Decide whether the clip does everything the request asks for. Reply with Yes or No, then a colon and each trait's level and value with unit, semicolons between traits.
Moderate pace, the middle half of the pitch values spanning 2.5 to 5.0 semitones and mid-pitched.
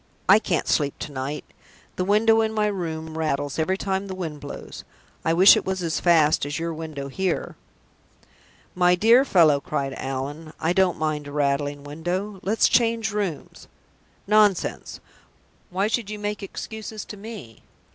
No: average, 160 wpm; wide, 5.5 semitones; medium, 175 Hz